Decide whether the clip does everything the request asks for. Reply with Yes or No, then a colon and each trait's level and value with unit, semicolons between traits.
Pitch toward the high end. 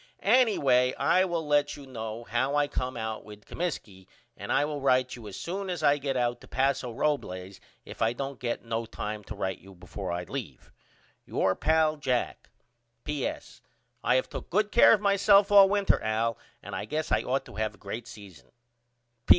No: low, 130 Hz